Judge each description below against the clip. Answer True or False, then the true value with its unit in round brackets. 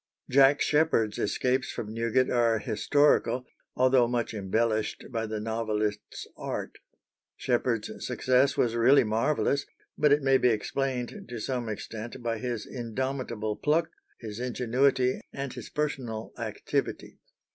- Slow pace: True (125 wpm)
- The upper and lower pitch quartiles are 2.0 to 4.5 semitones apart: True (3.0 semitones)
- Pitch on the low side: True (120 Hz)